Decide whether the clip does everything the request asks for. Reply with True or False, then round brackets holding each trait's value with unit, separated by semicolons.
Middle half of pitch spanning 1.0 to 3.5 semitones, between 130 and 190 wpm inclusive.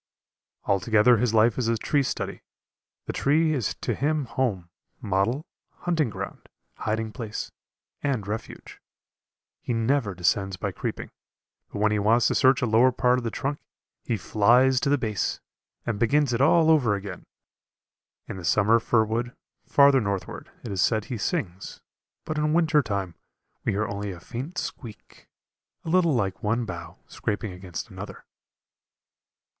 False (4.7 semitones; 160 wpm)